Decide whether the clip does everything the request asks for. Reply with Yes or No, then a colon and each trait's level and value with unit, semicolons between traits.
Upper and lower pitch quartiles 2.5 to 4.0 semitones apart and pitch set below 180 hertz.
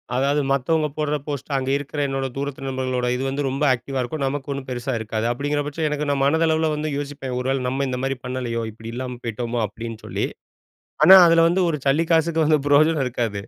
Yes: average, 2.9 semitones; low, 135 Hz